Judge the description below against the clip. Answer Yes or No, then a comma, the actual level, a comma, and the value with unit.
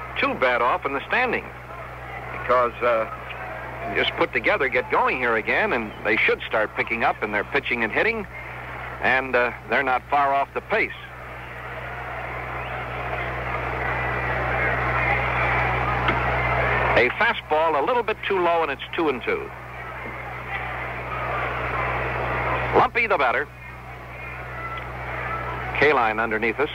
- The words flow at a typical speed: No, slow, 120 wpm